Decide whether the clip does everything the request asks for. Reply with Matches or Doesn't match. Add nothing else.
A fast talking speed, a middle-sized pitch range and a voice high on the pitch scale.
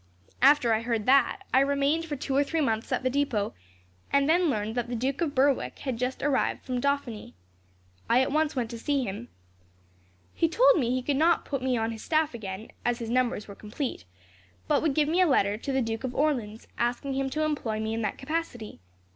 Matches